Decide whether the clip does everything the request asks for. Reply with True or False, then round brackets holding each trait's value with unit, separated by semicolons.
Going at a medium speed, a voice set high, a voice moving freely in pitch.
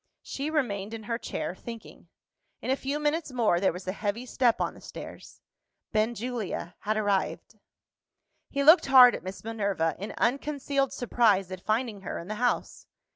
False (170 wpm; 225 Hz; 4.5 semitones)